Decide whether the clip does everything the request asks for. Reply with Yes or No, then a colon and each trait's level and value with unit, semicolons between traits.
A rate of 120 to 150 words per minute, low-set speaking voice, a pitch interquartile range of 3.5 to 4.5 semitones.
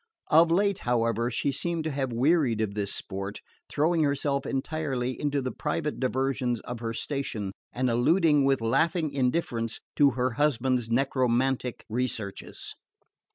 Yes: average, 140 wpm; low, 130 Hz; average, 3.9 semitones